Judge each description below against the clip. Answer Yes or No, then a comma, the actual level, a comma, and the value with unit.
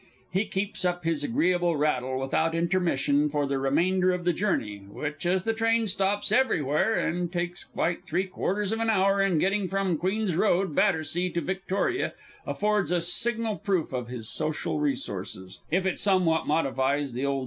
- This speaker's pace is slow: No, average, 175 wpm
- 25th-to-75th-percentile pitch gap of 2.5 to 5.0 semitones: Yes, average, 4.6 semitones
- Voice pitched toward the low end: No, medium, 175 Hz